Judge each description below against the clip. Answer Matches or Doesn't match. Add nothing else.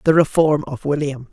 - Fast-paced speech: Doesn't match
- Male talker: Doesn't match